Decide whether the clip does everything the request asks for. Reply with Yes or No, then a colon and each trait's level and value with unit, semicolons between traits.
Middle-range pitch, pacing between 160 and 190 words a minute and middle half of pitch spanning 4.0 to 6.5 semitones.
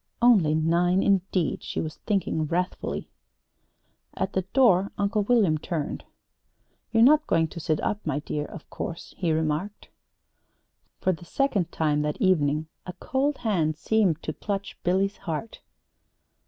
No: medium, 180 Hz; average, 140 wpm; average, 4.5 semitones